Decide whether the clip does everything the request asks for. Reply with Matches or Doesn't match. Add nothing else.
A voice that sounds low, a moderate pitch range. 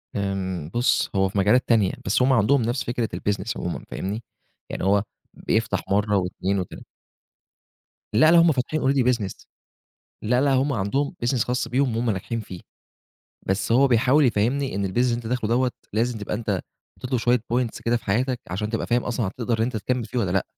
Matches